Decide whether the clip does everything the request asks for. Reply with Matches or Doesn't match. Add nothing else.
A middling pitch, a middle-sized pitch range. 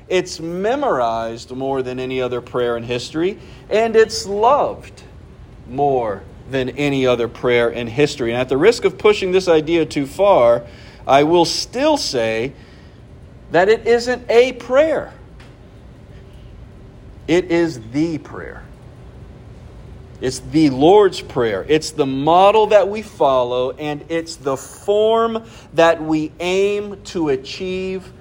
Doesn't match